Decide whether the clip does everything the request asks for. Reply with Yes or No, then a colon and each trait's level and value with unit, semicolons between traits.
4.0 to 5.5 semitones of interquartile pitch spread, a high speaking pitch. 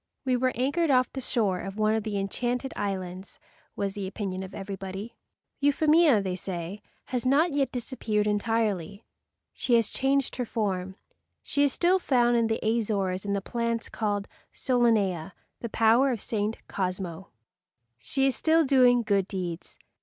Yes: average, 4.5 semitones; high, 220 Hz